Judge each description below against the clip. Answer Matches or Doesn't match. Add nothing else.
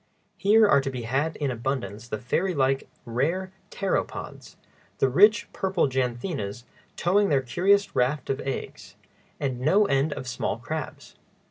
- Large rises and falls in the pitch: Matches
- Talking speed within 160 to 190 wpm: Doesn't match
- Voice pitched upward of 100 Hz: Matches